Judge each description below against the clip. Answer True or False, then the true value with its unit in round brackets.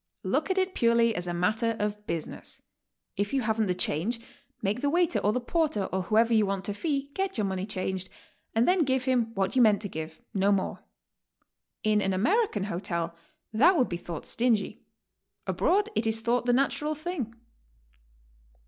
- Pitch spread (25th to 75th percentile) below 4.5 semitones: False (5.3 semitones)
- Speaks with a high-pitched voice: True (220 Hz)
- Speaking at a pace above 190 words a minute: False (185 wpm)